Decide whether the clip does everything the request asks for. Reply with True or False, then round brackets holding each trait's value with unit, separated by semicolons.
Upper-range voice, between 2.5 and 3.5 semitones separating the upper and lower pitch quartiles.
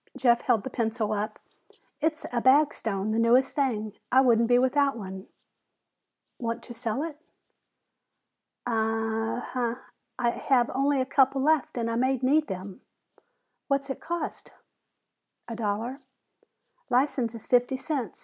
True (245 Hz; 3.2 semitones)